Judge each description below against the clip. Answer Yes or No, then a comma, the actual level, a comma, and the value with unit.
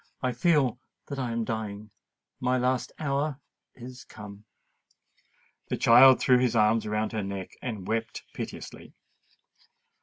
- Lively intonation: No, average, 3.1 semitones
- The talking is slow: Yes, slow, 130 wpm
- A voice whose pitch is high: No, low, 120 Hz